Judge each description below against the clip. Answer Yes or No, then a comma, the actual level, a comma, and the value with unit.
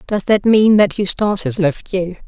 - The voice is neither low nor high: No, high, 195 Hz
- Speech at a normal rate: No, fast, 210 wpm